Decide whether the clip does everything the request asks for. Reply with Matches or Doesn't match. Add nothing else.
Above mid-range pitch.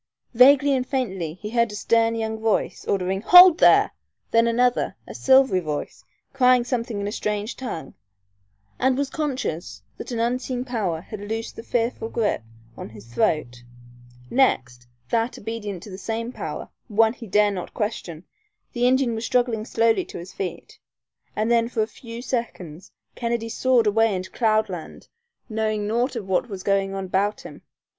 Matches